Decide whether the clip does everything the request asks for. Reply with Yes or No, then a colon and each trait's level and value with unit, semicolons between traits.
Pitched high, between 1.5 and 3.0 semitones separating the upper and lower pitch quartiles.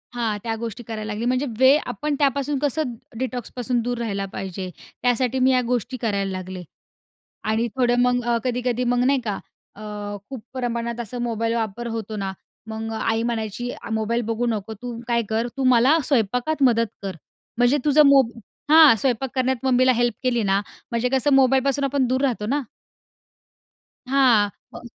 Yes: high, 240 Hz; narrow, 2.6 semitones